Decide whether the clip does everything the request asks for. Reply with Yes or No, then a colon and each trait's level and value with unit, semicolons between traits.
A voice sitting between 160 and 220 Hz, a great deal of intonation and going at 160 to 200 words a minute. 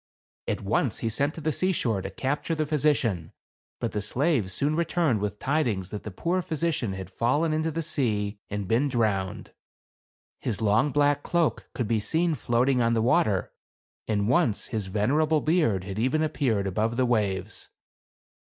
No: low, 120 Hz; wide, 6.7 semitones; average, 175 wpm